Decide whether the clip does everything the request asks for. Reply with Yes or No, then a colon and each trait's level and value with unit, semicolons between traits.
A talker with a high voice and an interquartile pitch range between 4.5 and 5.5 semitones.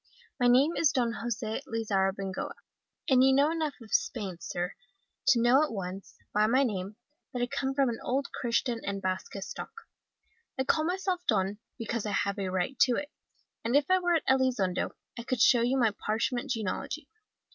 Yes: high, 240 Hz; average, 4.9 semitones